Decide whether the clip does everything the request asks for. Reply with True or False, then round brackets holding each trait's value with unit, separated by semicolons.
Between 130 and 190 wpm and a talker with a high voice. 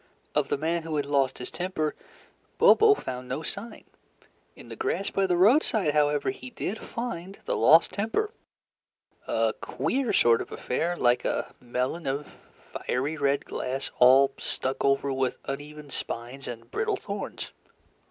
False (150 wpm; 150 Hz)